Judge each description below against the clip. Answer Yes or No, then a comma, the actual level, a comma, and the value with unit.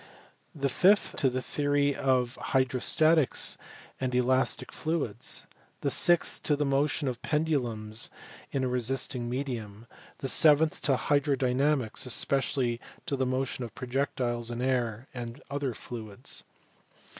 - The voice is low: Yes, low, 130 Hz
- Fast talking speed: No, slow, 135 wpm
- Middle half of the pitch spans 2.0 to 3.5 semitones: Yes, average, 2.8 semitones